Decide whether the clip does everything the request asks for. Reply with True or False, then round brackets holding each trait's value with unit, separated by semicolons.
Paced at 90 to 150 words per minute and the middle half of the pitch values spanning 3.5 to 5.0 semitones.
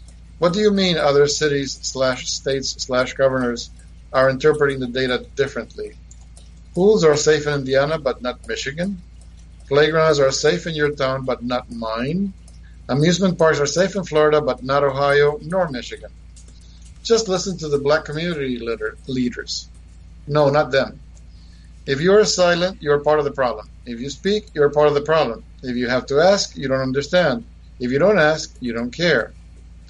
False (175 wpm; 4.2 semitones)